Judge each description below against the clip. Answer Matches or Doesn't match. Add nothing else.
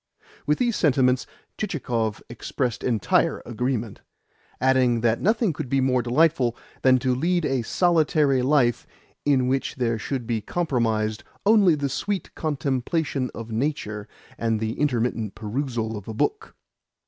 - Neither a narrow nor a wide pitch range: Matches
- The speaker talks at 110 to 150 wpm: Matches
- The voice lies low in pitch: Matches